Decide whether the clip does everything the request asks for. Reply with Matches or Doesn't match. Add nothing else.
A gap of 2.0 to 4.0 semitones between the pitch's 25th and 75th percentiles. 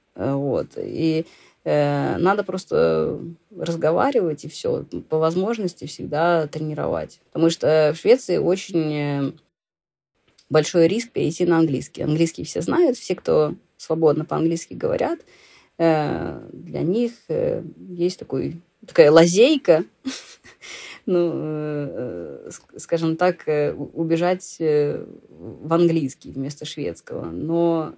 Matches